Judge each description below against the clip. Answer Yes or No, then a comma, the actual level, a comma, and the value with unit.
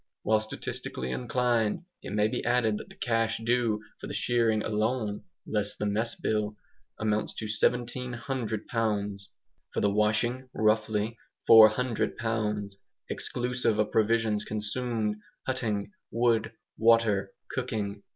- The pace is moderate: No, slow, 120 wpm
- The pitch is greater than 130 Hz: No, low, 110 Hz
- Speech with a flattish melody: Yes, narrow, 2.0 semitones